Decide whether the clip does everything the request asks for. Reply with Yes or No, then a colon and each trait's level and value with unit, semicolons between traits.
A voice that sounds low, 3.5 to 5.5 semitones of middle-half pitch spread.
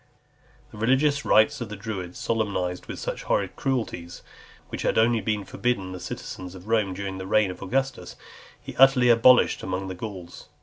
Yes: low, 105 Hz; average, 4.4 semitones